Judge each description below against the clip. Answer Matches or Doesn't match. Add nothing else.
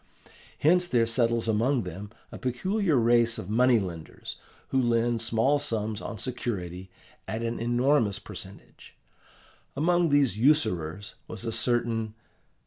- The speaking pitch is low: Matches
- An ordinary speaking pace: Doesn't match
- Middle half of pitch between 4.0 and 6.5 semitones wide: Doesn't match